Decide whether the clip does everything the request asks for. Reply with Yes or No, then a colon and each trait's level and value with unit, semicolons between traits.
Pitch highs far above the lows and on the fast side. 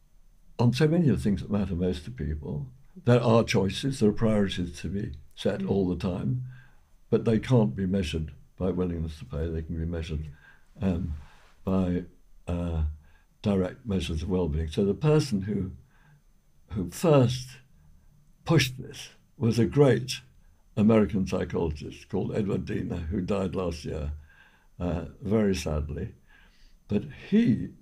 No: wide, 6.0 semitones; average, 150 wpm